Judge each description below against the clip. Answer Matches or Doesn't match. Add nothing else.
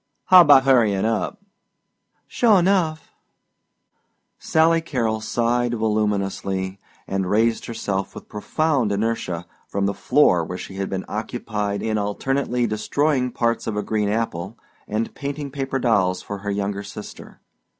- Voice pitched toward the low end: Matches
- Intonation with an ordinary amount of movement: Matches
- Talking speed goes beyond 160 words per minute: Doesn't match